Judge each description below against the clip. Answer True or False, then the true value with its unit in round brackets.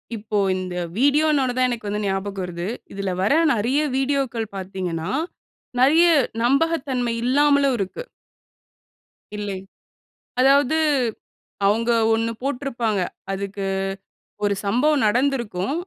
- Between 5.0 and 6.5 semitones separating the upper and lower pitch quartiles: True (5.6 semitones)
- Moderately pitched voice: False (235 Hz)